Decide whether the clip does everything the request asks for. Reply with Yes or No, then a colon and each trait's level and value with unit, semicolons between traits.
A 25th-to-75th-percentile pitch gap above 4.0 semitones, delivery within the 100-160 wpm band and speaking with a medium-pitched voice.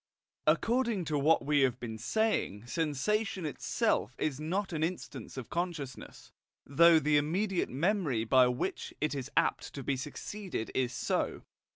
Yes: wide, 5.5 semitones; average, 150 wpm; medium, 150 Hz